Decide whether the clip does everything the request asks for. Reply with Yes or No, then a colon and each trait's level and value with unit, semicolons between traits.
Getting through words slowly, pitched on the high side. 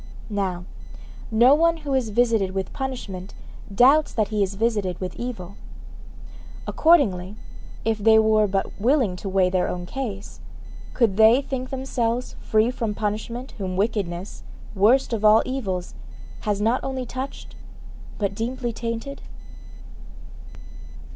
Yes: slow, 130 wpm; high, 220 Hz